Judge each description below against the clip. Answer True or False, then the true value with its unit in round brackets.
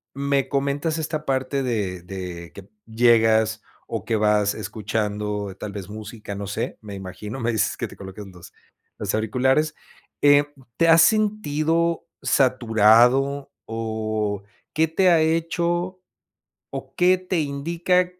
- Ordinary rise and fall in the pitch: False (6.9 semitones)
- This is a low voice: True (120 Hz)